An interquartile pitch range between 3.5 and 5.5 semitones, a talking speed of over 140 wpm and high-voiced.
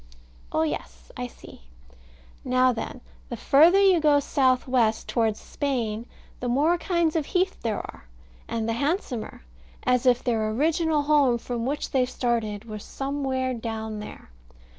Yes: average, 4.3 semitones; average, 150 wpm; very high, 250 Hz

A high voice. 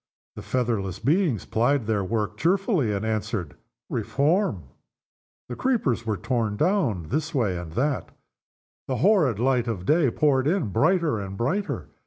No: low, 125 Hz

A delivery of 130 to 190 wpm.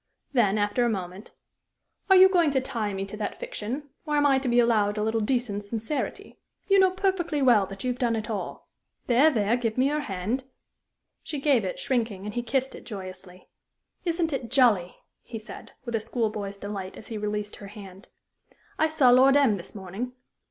No: average, 200 wpm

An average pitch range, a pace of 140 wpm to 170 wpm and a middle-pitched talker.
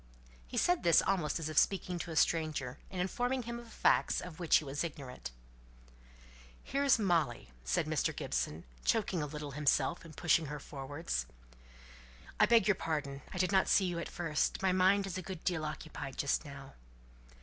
No: average, 4.6 semitones; average, 180 wpm; medium, 165 Hz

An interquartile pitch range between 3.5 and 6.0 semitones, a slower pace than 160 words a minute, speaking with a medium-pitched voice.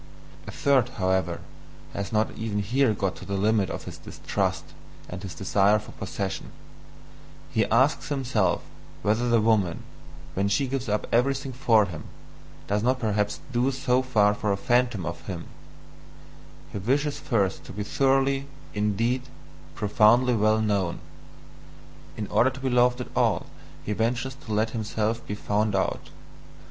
No: average, 3.8 semitones; average, 150 wpm; low, 110 Hz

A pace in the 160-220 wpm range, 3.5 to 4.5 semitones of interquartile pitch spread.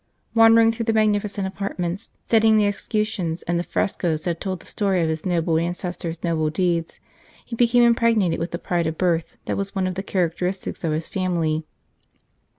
Yes: average, 185 wpm; average, 3.9 semitones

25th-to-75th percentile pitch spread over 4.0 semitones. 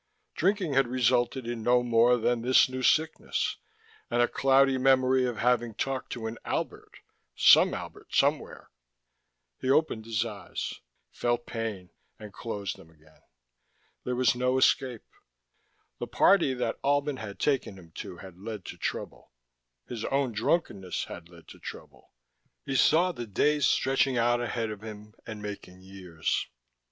No: average, 3.7 semitones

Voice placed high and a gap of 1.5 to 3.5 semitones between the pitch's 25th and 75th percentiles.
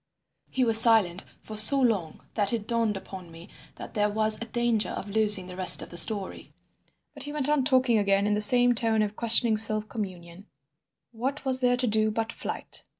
Yes: high, 220 Hz; average, 2.8 semitones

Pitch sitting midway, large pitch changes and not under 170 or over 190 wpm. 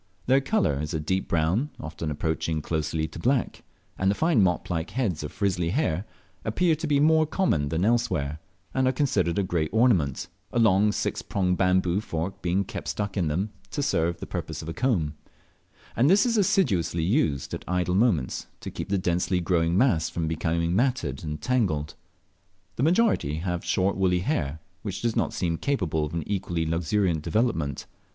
No: very low, 90 Hz; wide, 6.3 semitones; average, 185 wpm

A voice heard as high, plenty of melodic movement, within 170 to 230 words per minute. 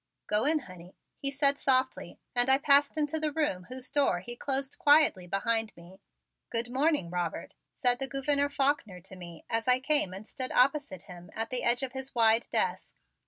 Yes: very high, 255 Hz; wide, 6.1 semitones; average, 190 wpm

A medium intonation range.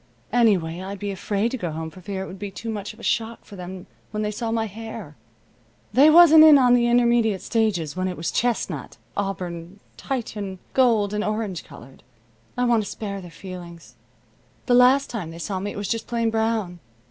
Yes: average, 3.9 semitones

